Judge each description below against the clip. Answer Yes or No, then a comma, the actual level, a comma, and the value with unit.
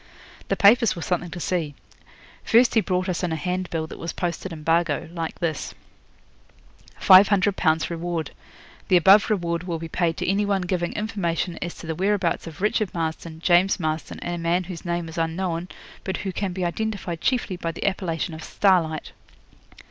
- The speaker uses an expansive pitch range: No, narrow, 2.5 semitones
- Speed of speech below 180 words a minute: No, average, 185 wpm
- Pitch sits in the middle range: Yes, medium, 175 Hz